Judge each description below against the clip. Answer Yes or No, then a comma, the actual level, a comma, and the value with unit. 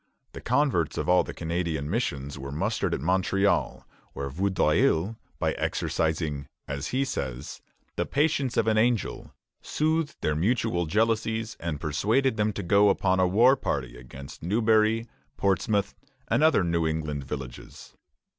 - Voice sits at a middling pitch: No, very low, 95 Hz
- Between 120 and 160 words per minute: Yes, average, 145 wpm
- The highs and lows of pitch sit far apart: Yes, wide, 6.8 semitones